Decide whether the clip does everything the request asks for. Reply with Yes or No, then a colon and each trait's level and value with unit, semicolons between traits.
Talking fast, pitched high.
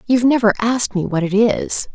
Yes: fast, 215 wpm; high, 220 Hz